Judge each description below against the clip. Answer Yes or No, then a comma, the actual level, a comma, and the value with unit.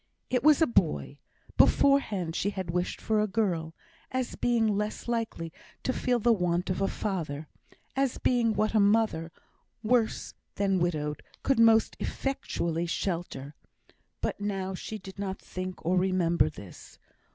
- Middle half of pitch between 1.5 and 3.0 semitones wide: No, average, 4.7 semitones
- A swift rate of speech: No, average, 150 wpm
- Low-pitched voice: No, high, 195 Hz